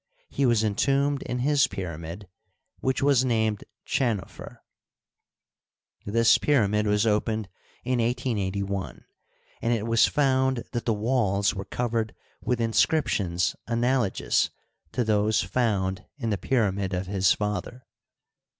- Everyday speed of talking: No, slow, 120 wpm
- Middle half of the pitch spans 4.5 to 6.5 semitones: No, average, 3.8 semitones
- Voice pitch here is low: Yes, low, 110 Hz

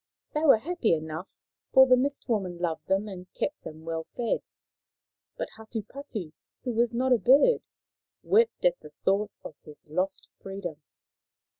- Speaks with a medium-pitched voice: No, high, 215 Hz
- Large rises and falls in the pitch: Yes, wide, 6.8 semitones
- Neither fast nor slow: Yes, average, 155 wpm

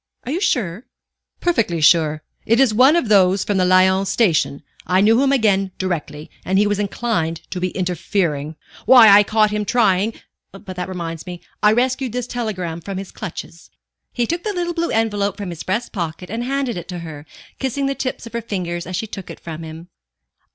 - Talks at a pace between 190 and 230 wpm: Yes, average, 200 wpm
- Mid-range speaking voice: No, high, 200 Hz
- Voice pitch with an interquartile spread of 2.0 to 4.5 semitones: No, average, 4.9 semitones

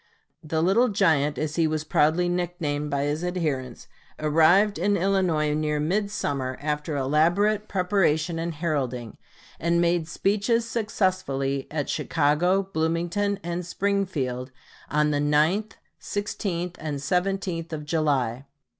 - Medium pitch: Yes, medium, 165 Hz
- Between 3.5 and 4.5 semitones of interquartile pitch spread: Yes, average, 4.1 semitones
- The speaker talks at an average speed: No, slow, 120 wpm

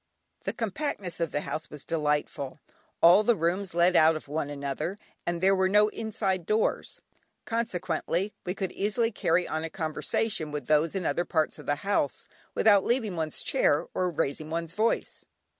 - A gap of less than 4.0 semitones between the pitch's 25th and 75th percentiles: No, average, 4.4 semitones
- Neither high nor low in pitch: Yes, medium, 175 Hz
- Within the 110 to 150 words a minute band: No, average, 175 wpm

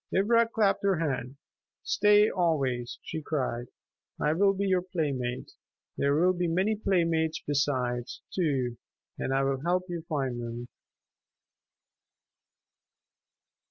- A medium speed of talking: No, slow, 120 wpm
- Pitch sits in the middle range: Yes, medium, 160 Hz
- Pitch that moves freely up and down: Yes, wide, 5.8 semitones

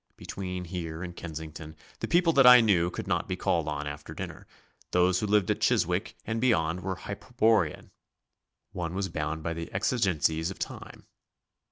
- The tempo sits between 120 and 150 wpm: No, average, 170 wpm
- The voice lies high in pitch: No, very low, 90 Hz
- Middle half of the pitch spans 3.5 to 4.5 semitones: Yes, average, 4.1 semitones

